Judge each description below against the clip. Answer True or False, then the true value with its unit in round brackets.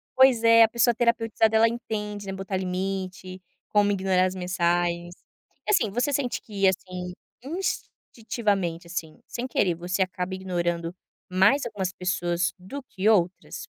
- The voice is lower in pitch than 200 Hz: True (190 Hz)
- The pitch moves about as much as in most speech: True (3.7 semitones)